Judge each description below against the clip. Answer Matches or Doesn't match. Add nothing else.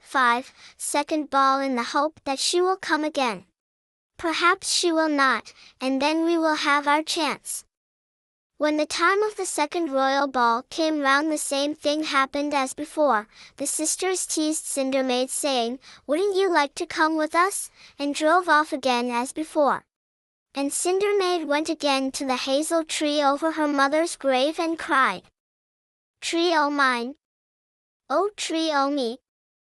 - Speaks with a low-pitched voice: Doesn't match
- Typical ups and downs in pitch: Matches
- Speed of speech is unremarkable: Matches